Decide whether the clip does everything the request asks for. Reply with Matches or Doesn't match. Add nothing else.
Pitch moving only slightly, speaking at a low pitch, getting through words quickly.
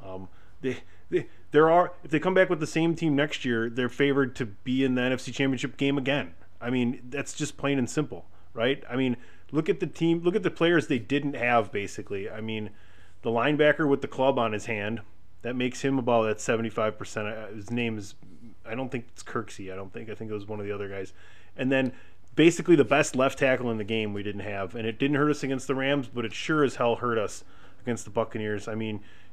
Doesn't match